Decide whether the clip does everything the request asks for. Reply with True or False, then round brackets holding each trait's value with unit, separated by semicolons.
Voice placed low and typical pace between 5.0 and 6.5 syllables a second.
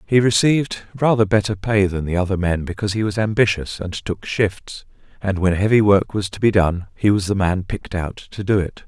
True (100 Hz; 5.5 syllables/s)